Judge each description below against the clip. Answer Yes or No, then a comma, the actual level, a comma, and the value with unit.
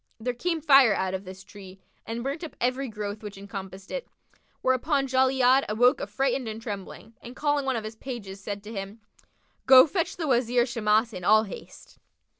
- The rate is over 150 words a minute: Yes, average, 185 wpm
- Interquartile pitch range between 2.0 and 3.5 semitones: No, average, 4.5 semitones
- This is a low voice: No, high, 230 Hz